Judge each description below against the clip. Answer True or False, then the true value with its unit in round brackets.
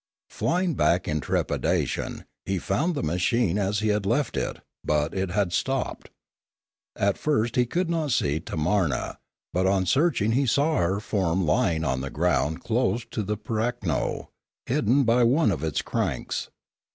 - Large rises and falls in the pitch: True (6.4 semitones)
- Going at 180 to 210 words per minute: False (160 wpm)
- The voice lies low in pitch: True (105 Hz)